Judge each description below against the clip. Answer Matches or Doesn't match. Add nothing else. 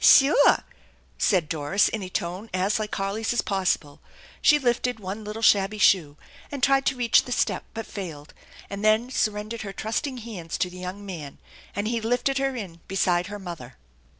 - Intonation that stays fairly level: Doesn't match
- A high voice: Matches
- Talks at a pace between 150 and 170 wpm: Doesn't match